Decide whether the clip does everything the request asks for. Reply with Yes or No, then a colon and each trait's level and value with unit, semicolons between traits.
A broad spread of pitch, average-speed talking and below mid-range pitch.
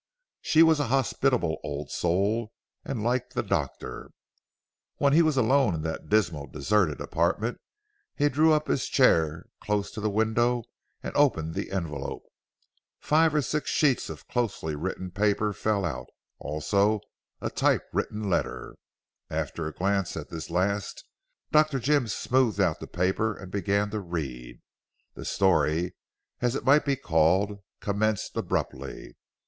Yes: wide, 6.8 semitones; average, 145 wpm; low, 105 Hz